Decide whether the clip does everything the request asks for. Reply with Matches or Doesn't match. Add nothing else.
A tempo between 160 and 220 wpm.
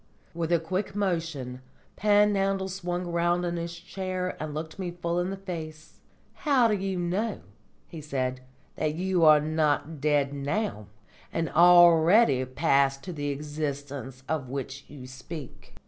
Doesn't match